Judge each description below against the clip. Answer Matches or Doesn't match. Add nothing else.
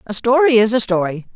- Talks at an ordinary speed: Doesn't match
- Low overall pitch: Doesn't match